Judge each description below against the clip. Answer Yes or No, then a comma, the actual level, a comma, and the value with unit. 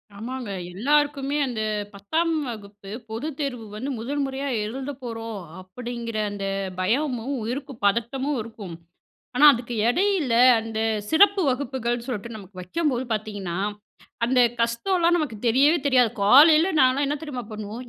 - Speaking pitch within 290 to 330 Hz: No, high, 245 Hz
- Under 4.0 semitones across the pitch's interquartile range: No, average, 4.4 semitones